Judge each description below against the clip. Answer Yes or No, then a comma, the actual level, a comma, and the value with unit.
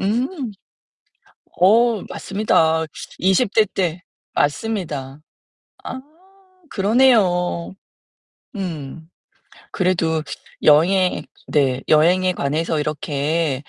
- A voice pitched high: No, medium, 175 Hz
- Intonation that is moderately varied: Yes, average, 4.6 semitones